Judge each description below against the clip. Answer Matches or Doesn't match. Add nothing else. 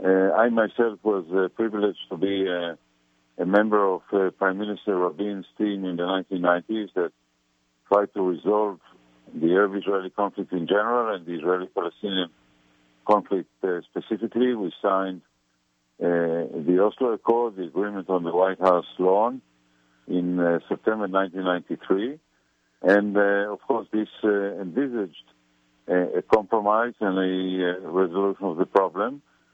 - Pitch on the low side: Matches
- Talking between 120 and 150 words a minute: Matches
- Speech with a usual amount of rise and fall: Matches